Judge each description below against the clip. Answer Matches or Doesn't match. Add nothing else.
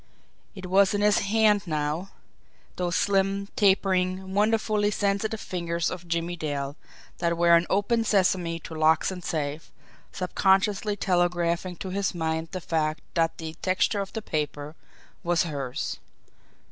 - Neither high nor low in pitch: Matches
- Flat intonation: Doesn't match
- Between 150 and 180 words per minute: Doesn't match